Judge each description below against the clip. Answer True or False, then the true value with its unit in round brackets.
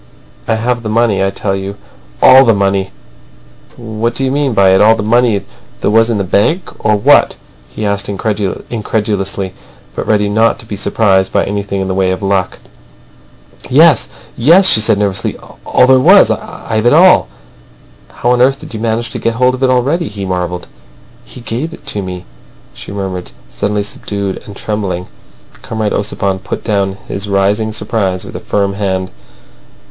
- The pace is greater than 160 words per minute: True (180 wpm)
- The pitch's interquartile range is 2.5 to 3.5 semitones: True (3.0 semitones)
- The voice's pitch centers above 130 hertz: False (105 Hz)